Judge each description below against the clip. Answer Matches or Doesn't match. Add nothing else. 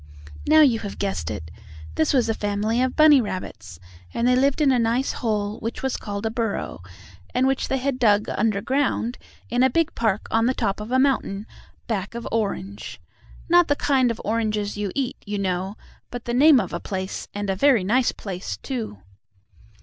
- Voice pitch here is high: Matches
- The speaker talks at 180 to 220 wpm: Matches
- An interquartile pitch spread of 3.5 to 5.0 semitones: Matches